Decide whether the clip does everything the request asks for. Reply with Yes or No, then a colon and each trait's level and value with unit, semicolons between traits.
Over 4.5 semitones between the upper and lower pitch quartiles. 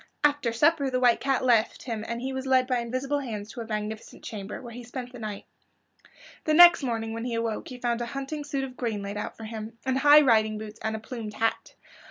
No: average, 3.2 semitones